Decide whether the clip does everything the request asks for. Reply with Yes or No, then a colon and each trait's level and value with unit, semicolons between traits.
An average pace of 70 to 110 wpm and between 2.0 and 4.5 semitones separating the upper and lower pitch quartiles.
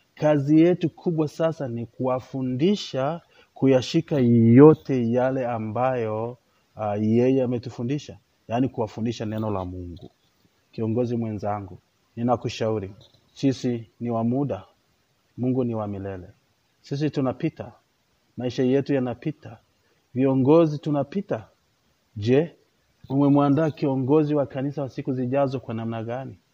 Yes: average, 105 wpm; average, 3.7 semitones